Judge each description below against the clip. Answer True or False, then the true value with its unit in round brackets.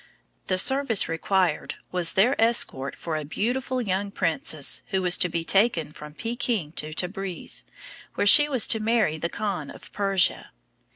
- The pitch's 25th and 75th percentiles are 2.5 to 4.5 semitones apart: False (5.5 semitones)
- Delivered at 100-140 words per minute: False (160 wpm)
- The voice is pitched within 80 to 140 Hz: False (190 Hz)